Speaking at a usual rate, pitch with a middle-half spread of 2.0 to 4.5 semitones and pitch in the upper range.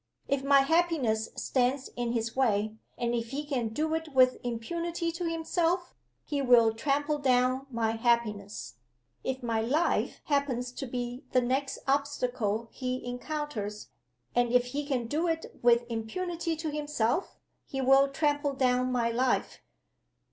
Yes: average, 150 wpm; average, 3.7 semitones; very high, 255 Hz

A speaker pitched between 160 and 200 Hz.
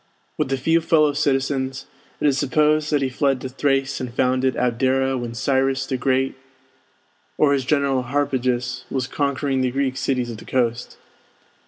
No: low, 135 Hz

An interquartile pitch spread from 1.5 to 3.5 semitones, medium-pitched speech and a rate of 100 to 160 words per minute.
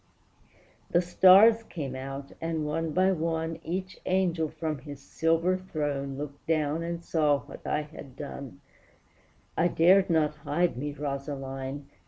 Yes: average, 3.2 semitones; medium, 155 Hz; average, 140 wpm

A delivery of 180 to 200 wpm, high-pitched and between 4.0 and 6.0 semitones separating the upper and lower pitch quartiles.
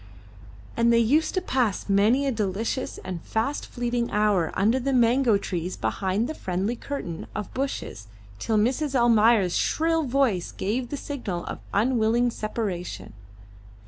No: average, 145 wpm; high, 230 Hz; average, 4.6 semitones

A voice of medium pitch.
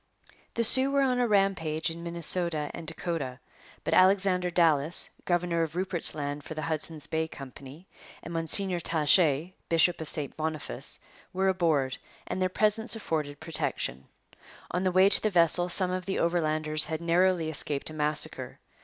Yes: medium, 170 Hz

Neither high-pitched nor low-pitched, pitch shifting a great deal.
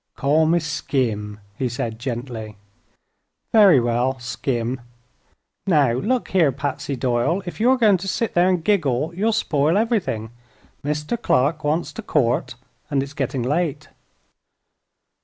Yes: medium, 145 Hz; wide, 6.1 semitones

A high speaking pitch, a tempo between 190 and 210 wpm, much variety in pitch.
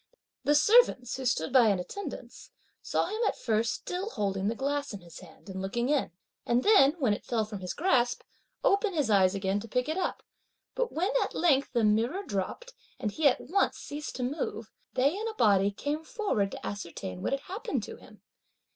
Yes: very high, 250 Hz; fast, 205 wpm; wide, 7.8 semitones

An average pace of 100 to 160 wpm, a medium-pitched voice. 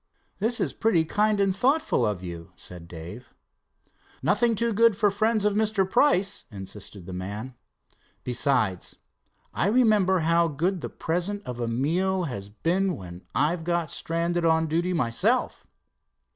Yes: average, 145 wpm; medium, 170 Hz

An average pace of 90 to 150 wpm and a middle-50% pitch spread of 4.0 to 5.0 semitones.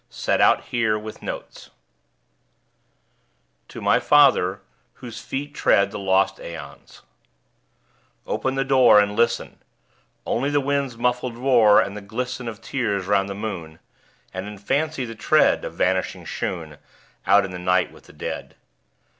Yes: average, 145 wpm; average, 4.5 semitones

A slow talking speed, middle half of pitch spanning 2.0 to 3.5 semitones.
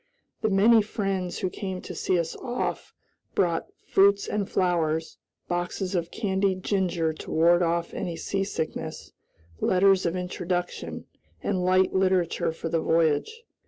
Yes: slow, 130 wpm; narrow, 2.4 semitones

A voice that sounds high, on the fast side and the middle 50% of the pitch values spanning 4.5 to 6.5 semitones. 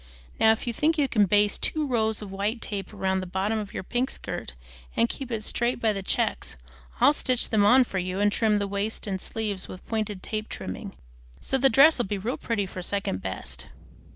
No: high, 210 Hz; fast, 215 wpm; average, 3.3 semitones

